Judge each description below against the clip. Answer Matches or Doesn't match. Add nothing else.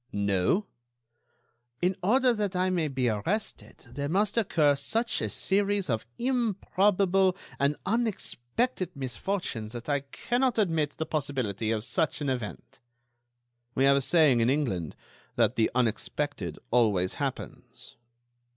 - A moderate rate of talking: Doesn't match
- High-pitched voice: Doesn't match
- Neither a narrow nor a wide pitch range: Doesn't match